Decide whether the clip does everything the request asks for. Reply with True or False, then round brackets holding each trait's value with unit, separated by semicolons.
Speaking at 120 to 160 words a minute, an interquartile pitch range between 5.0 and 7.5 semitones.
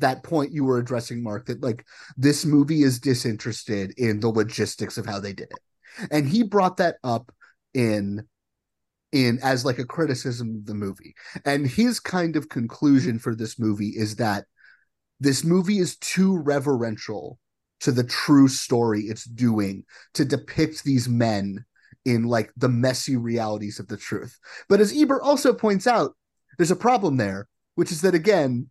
False (170 wpm; 5.4 semitones)